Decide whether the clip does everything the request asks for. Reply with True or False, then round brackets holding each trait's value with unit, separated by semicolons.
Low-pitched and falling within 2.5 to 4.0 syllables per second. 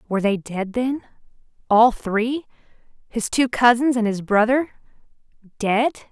False (230 Hz; 3.9 syllables/s)